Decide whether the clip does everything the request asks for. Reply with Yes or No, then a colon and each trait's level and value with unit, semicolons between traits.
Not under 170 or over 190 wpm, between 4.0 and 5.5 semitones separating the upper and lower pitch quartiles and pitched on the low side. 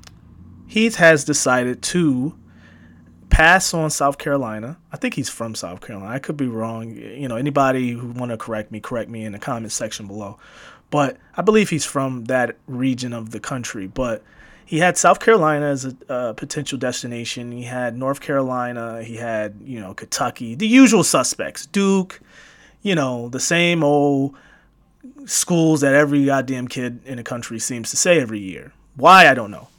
Yes: average, 175 wpm; average, 4.7 semitones; low, 130 Hz